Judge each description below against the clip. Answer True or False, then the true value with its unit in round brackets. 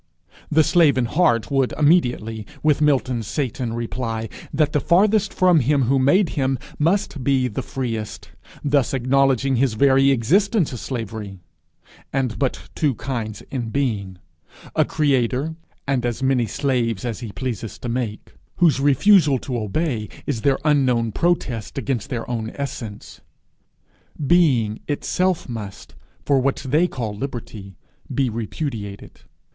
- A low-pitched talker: True (130 Hz)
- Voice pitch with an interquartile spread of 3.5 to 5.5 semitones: True (4.0 semitones)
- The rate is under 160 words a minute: True (140 wpm)